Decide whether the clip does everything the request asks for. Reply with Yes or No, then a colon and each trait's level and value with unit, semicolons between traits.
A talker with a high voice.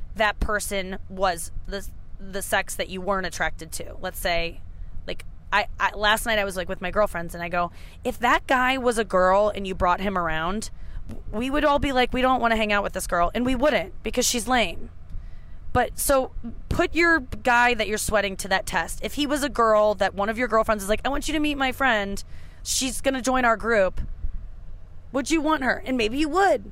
Yes: high, 210 Hz